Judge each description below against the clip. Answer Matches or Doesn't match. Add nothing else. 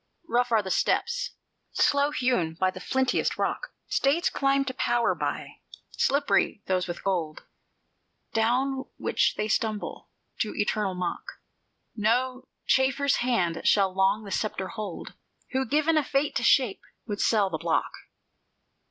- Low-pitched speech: Doesn't match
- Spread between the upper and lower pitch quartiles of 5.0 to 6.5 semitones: Matches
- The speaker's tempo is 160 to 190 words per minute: Doesn't match